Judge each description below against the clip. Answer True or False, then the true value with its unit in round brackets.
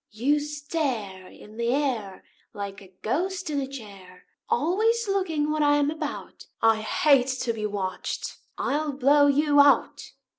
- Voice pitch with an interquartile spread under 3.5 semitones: False (5.6 semitones)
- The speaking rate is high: False (150 wpm)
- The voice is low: False (280 Hz)